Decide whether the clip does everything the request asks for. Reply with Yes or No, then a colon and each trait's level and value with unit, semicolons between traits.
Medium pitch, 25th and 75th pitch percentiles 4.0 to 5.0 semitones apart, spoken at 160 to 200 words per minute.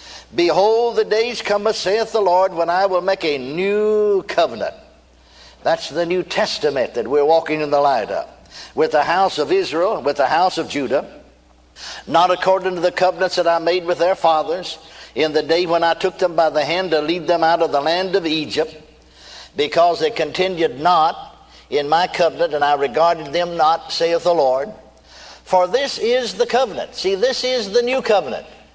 Yes: medium, 175 Hz; average, 4.3 semitones; average, 190 wpm